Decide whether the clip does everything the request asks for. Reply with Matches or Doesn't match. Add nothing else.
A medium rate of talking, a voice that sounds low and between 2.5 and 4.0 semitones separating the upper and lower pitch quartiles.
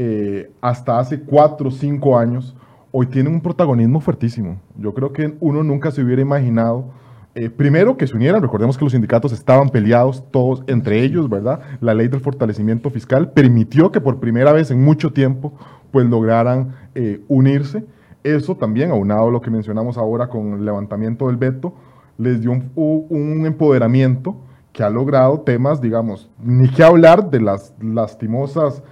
Matches